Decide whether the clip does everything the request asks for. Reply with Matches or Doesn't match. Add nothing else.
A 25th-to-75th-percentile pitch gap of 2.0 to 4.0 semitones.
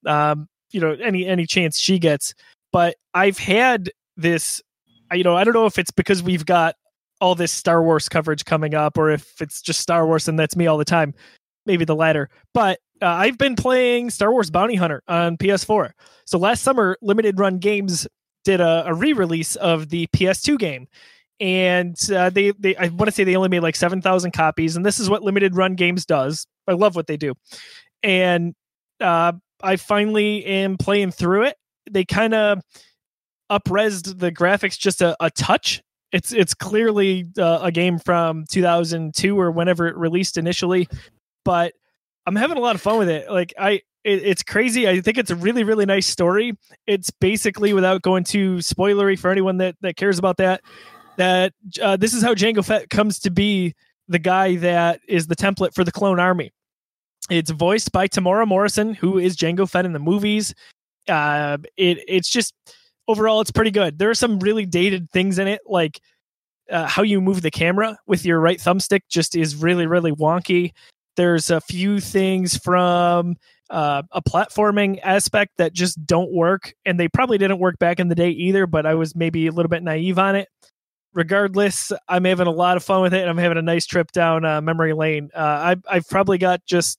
Matches